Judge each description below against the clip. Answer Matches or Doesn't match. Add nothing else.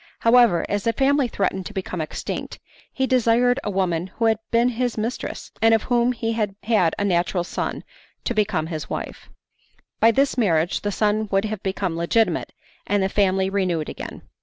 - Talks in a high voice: Matches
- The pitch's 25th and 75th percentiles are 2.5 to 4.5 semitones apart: Matches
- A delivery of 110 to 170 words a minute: Doesn't match